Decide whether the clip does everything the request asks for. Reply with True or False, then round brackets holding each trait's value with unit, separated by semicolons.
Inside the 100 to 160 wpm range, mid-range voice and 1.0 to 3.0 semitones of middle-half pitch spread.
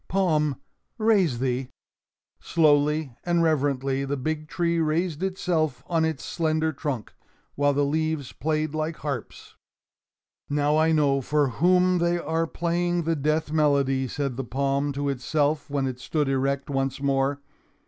True (145 wpm; 150 Hz; 2.7 semitones)